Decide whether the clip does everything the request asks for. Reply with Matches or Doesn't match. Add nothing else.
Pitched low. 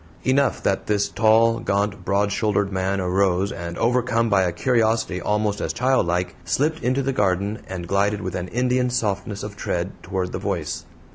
Matches